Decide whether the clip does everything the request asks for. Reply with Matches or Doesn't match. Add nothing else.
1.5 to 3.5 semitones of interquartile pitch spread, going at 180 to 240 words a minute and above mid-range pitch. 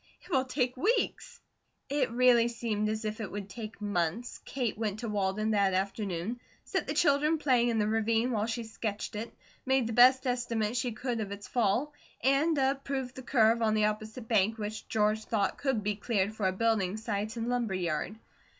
Matches